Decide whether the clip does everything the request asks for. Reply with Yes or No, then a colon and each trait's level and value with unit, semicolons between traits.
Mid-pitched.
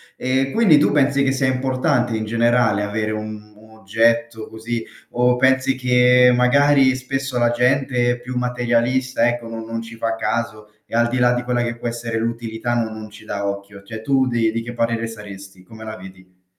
No: low, 120 Hz